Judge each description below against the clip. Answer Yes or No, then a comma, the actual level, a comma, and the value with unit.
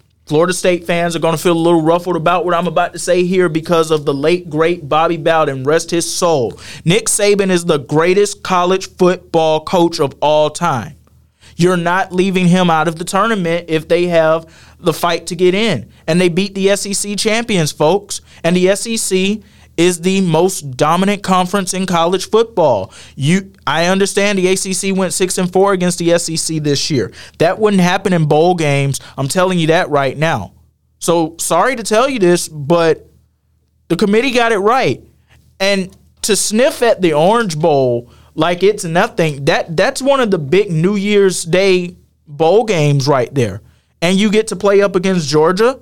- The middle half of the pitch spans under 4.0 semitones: Yes, average, 3.1 semitones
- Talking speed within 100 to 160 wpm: No, average, 185 wpm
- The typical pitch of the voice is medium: Yes, medium, 175 Hz